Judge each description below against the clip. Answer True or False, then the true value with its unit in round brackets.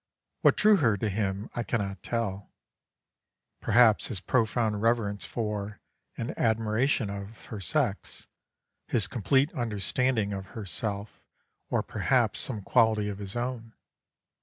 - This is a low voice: True (110 Hz)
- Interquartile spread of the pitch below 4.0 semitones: True (2.7 semitones)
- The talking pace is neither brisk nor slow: False (125 wpm)